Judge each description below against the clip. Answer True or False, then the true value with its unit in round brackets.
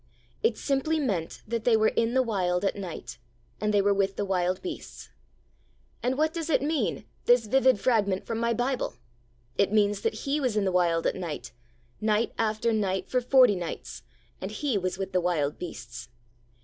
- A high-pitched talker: True (210 Hz)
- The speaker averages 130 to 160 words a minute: False (190 wpm)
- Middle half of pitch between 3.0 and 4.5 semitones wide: False (5.0 semitones)